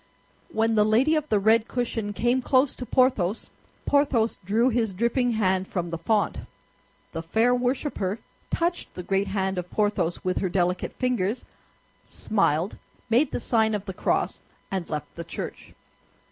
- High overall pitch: Yes, high, 215 Hz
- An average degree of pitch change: Yes, average, 4.6 semitones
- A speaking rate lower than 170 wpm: Yes, average, 160 wpm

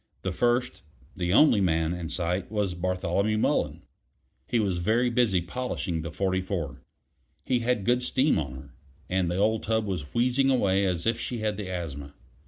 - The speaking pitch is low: Yes, very low, 95 Hz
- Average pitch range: Yes, average, 4.9 semitones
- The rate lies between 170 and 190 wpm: Yes, average, 175 wpm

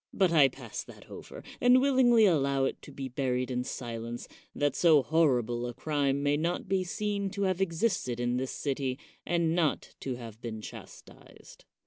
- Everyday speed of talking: Yes, average, 175 wpm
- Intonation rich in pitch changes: Yes, wide, 6.0 semitones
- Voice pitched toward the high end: No, medium, 140 Hz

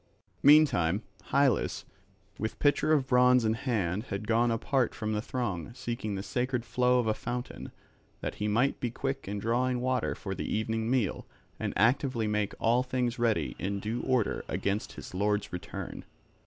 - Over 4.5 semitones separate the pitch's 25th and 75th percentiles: No, average, 3.2 semitones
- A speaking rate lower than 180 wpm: Yes, average, 170 wpm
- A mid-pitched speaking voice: No, low, 115 Hz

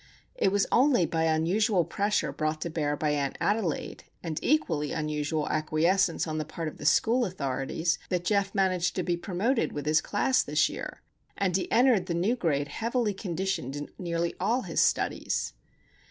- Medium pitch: Yes, medium, 175 Hz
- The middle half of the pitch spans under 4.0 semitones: No, average, 4.6 semitones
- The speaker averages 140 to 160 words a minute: No, average, 175 wpm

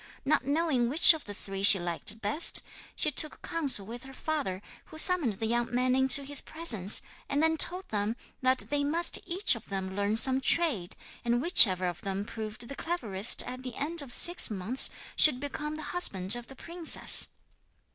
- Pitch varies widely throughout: Yes, wide, 6.8 semitones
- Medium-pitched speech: No, very high, 255 Hz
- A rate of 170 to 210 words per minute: Yes, average, 185 wpm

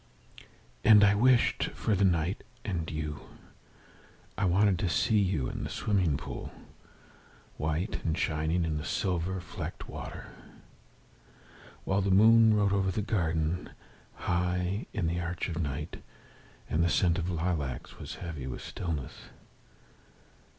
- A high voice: No, very low, 90 Hz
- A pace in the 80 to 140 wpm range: Yes, slow, 135 wpm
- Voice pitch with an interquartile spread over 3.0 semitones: Yes, average, 3.6 semitones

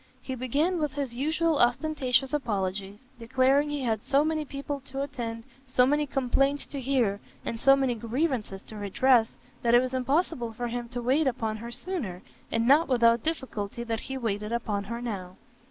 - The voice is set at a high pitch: Yes, very high, 250 Hz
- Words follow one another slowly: No, average, 180 wpm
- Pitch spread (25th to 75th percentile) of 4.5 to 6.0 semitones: No, average, 3.5 semitones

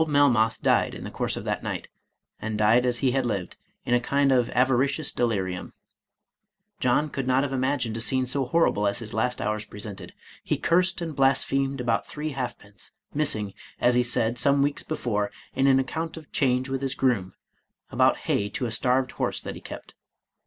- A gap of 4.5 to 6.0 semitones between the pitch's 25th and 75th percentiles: No, average, 3.5 semitones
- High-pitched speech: No, low, 125 Hz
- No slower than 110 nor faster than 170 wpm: No, average, 195 wpm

